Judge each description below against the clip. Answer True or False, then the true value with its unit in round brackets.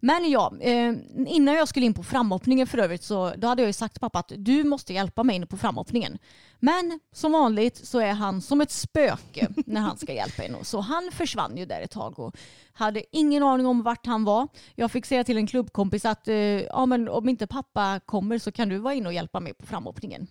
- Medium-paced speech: False (225 wpm)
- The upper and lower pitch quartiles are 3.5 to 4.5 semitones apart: True (3.9 semitones)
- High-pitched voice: True (240 Hz)